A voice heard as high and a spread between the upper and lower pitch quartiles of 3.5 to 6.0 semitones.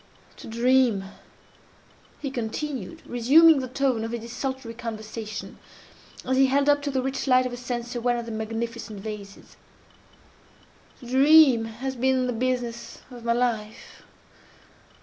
No: high, 245 Hz; narrow, 2.5 semitones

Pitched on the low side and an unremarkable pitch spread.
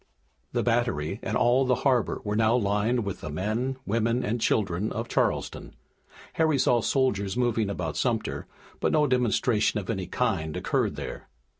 Yes: low, 115 Hz; average, 3.7 semitones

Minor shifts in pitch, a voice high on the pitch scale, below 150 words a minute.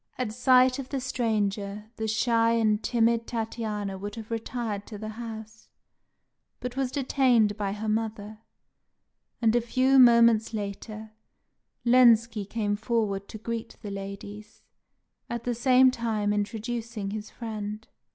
Yes: narrow, 2.1 semitones; high, 225 Hz; slow, 135 wpm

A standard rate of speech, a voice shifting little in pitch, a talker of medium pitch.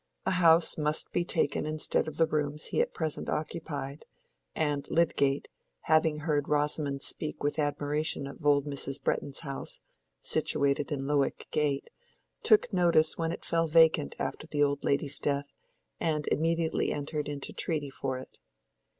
Yes: average, 150 wpm; narrow, 2.1 semitones; medium, 150 Hz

